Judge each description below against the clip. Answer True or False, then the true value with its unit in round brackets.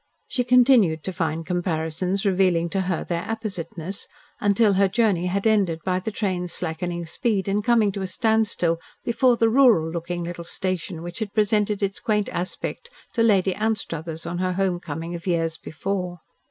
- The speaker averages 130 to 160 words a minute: False (170 wpm)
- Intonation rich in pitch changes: False (3.6 semitones)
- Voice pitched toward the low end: False (185 Hz)